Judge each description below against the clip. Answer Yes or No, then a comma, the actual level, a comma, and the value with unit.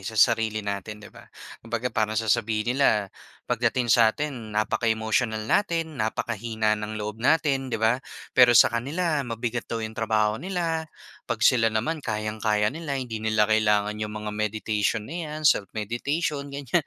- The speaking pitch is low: Yes, low, 115 Hz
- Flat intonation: No, average, 3.4 semitones